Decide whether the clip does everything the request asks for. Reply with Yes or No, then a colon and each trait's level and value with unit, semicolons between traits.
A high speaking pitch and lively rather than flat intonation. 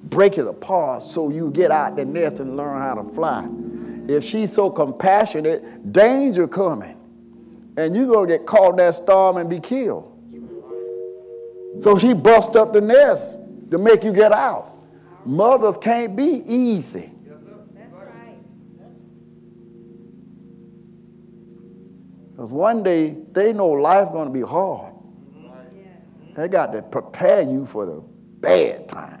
Yes: high, 195 Hz; wide, 6.5 semitones